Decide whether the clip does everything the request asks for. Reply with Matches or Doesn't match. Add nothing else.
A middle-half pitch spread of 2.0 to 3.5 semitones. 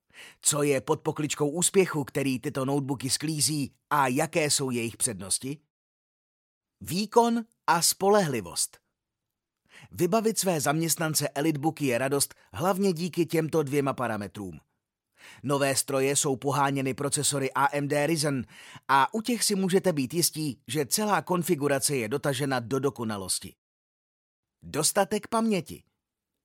Doesn't match